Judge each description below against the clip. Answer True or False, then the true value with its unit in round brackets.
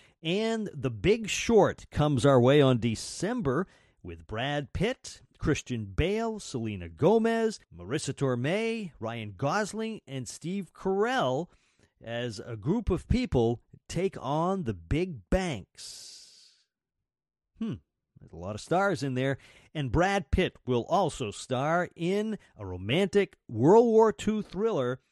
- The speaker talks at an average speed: False (130 wpm)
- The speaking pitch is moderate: True (145 Hz)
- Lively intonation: True (8.6 semitones)